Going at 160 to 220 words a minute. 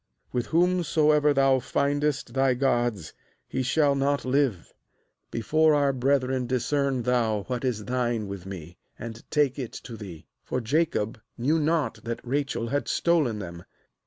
No: average, 150 wpm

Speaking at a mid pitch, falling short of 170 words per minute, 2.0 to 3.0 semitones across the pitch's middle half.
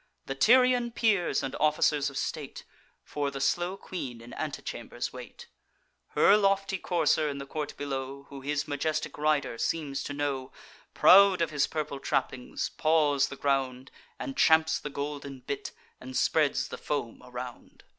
Yes: medium, 145 Hz; average, 155 wpm; average, 2.7 semitones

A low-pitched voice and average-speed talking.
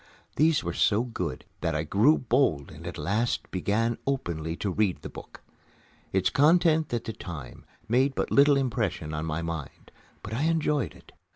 Yes: low, 110 Hz; average, 175 wpm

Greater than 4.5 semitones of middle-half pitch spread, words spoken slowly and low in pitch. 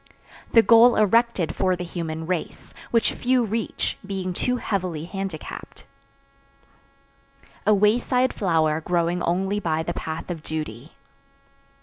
No: average, 5.1 semitones; slow, 120 wpm; medium, 185 Hz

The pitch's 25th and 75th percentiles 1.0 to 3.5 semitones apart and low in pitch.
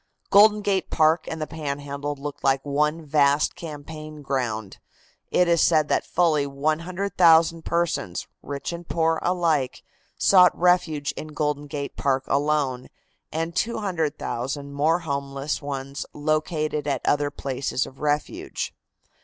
No: average, 2.7 semitones; medium, 150 Hz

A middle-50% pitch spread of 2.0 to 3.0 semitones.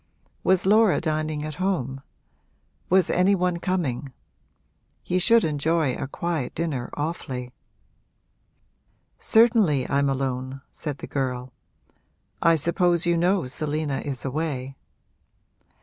No: average, 4.6 semitones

